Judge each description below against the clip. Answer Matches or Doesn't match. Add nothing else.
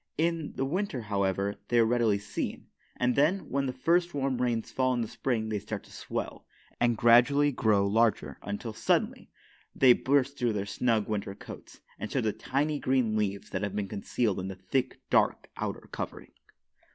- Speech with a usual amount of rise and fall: Matches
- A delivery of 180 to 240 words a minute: Matches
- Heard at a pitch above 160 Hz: Doesn't match